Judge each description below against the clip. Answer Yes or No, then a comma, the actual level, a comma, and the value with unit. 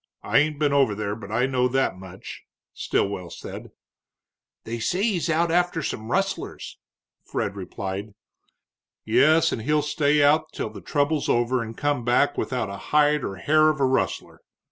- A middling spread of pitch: No, wide, 5.7 semitones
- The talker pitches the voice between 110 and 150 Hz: Yes, low, 135 Hz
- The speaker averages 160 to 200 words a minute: Yes, average, 165 wpm